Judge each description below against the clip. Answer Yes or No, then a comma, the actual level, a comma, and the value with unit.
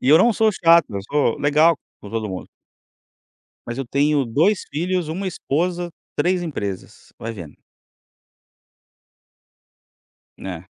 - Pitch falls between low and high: Yes, medium, 150 Hz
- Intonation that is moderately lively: No, wide, 7.3 semitones